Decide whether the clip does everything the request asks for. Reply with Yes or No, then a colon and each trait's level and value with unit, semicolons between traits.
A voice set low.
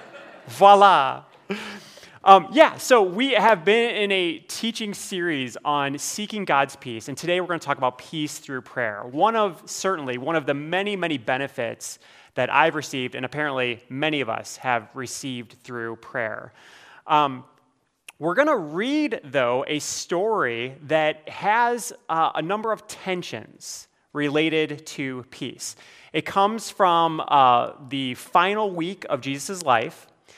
No: medium, 155 Hz